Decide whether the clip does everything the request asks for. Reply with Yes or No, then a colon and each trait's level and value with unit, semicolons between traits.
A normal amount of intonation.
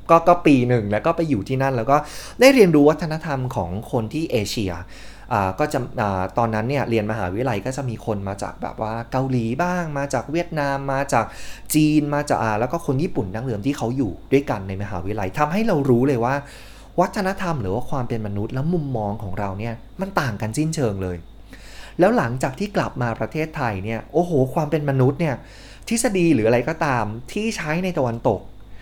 No: wide, 5.8 semitones